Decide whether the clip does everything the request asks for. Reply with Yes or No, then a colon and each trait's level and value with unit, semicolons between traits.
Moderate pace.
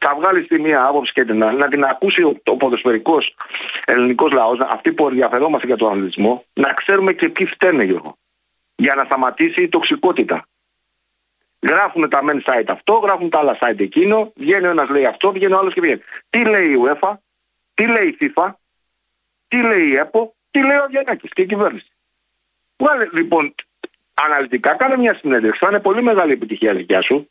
No: fast, 180 wpm